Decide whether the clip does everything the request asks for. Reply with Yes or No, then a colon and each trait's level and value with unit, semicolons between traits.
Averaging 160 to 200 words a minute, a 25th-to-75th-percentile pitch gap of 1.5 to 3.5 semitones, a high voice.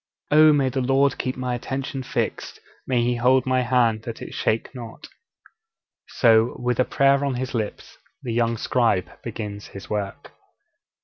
No: average, 165 wpm; narrow, 2.4 semitones; low, 125 Hz